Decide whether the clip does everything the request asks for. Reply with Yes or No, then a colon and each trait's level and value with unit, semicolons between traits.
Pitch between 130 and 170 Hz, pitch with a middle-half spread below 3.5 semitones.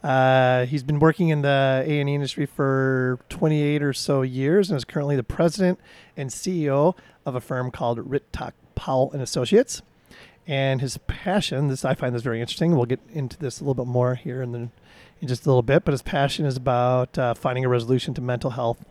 Yes: low, 135 Hz; average, 2.8 semitones